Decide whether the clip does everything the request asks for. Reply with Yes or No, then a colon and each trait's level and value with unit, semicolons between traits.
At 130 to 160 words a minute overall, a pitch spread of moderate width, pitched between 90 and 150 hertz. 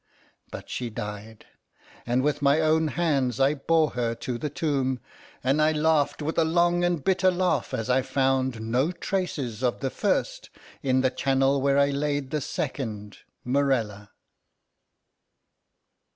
Yes: average, 150 wpm; average, 3.6 semitones; low, 135 Hz